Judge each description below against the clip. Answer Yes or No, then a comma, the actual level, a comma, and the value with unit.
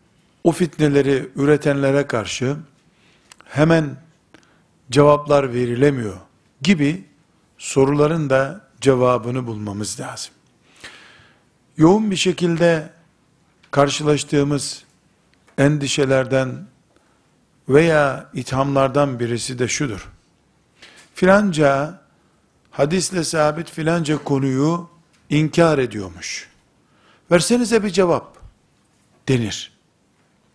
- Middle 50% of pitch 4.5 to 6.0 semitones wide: No, average, 3.7 semitones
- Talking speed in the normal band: No, slow, 65 wpm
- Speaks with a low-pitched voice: No, medium, 145 Hz